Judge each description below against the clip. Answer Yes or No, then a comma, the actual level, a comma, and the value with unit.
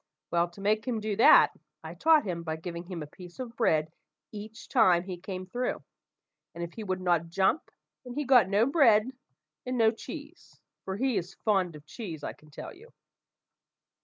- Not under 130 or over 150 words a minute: No, average, 190 wpm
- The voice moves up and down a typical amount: No, wide, 5.8 semitones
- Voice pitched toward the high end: Yes, high, 200 Hz